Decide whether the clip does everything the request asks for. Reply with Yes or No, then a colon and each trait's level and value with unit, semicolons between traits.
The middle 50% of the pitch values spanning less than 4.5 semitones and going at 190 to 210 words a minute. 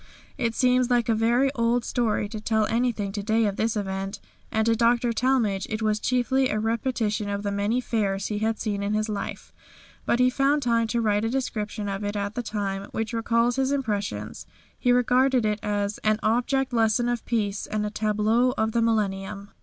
Yes: narrow, 2.6 semitones; average, 200 wpm